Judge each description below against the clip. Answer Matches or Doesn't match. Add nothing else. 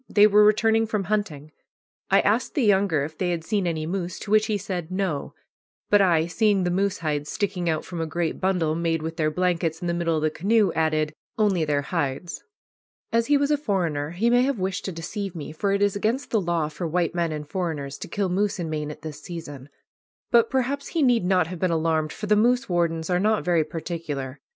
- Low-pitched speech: Doesn't match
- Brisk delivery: Matches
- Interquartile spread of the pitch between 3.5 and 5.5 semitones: Matches